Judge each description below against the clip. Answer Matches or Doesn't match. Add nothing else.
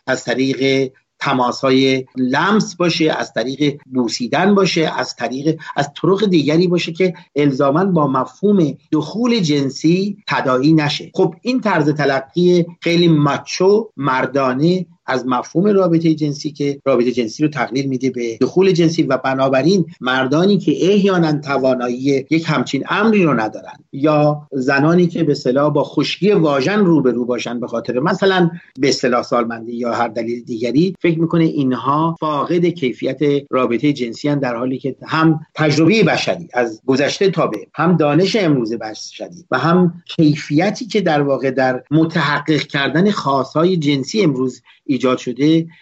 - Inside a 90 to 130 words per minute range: Doesn't match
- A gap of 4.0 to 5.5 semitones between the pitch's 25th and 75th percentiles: Matches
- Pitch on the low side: Doesn't match